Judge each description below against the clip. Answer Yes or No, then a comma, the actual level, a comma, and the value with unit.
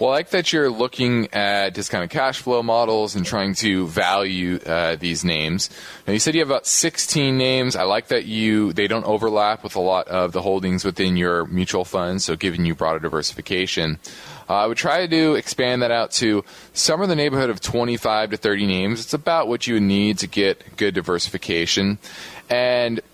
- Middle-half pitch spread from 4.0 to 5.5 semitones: Yes, average, 4.6 semitones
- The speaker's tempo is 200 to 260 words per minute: Yes, fast, 205 wpm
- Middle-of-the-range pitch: No, low, 105 Hz